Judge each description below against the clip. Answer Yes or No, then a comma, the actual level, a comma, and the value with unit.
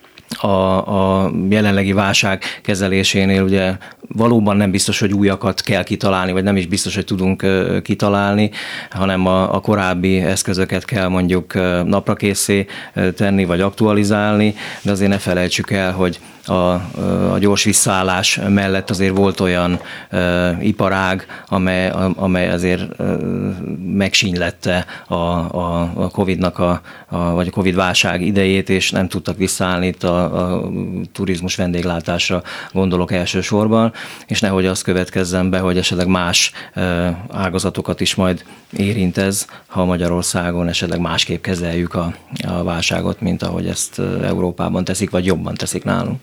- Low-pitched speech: Yes, very low, 95 Hz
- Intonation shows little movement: Yes, narrow, 1.8 semitones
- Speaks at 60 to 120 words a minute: No, average, 140 wpm